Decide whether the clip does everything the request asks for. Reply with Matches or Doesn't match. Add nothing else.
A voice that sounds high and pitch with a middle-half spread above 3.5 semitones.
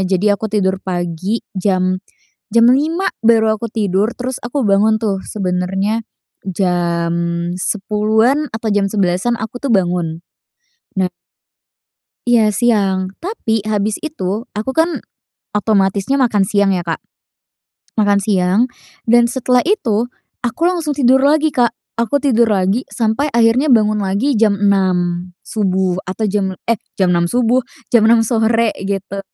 Matches